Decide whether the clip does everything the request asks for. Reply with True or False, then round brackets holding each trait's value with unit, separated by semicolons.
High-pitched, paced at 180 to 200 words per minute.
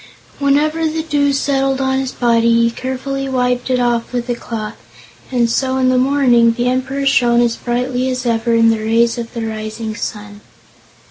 True (245 Hz; 185 wpm)